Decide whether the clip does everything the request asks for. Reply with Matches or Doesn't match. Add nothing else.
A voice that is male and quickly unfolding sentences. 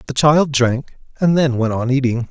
Matches